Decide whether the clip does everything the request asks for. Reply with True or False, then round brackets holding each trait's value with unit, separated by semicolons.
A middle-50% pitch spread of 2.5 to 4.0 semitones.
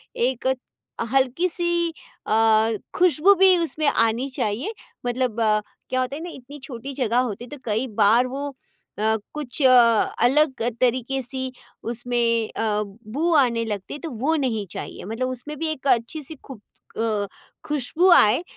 False (4.5 semitones)